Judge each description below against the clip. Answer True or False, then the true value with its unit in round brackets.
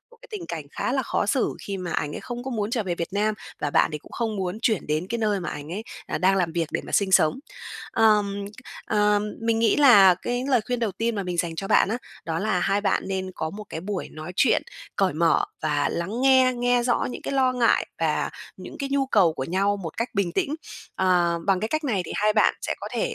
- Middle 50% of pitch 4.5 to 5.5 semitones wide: True (5.1 semitones)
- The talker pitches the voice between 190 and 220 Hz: True (205 Hz)